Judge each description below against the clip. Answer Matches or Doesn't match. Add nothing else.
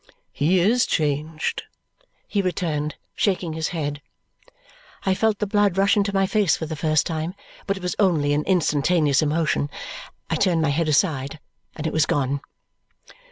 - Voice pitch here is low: Doesn't match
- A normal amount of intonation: Matches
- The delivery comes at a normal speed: Matches